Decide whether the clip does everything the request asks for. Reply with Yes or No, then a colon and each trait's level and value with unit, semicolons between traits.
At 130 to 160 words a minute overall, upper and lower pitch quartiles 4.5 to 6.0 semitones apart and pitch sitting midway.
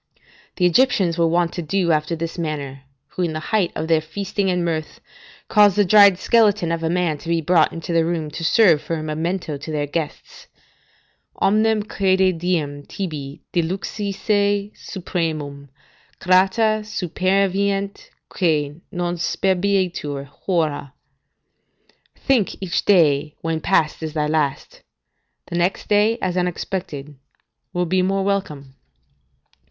No: average, 140 wpm; average, 3.8 semitones; medium, 175 Hz